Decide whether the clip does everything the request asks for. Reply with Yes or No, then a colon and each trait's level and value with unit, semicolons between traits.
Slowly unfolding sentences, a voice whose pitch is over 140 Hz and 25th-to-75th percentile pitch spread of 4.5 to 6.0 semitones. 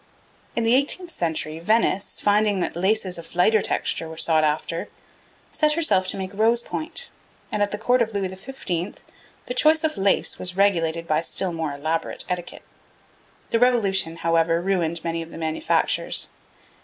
No: average, 165 wpm; high, 190 Hz; average, 5.0 semitones